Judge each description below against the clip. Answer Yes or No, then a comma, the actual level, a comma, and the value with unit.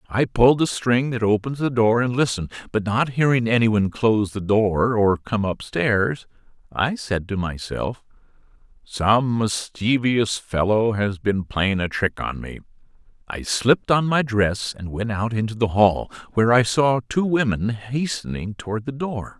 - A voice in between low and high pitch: No, low, 115 Hz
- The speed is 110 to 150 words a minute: No, average, 170 wpm